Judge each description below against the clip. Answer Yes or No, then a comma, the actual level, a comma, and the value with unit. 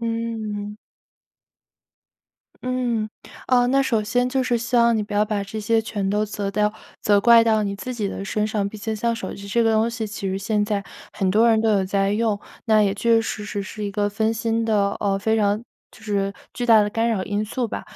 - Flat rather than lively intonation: Yes, narrow, 2.0 semitones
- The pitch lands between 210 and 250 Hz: Yes, high, 215 Hz